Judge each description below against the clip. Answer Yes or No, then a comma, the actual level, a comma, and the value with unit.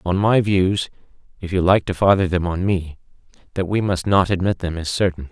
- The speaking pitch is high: No, very low, 90 Hz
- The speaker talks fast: Yes, fast, 215 wpm